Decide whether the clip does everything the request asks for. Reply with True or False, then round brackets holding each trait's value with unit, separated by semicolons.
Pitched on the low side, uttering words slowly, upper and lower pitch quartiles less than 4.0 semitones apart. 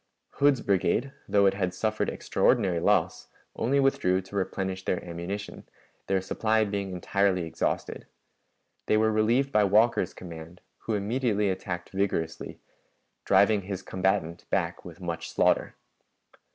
True (100 Hz; 130 wpm; 2.9 semitones)